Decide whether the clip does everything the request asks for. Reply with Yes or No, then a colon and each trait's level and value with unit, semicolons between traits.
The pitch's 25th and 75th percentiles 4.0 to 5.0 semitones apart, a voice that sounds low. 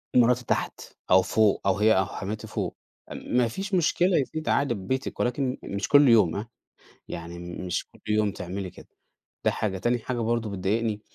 Yes: average, 4.5 semitones; low, 110 Hz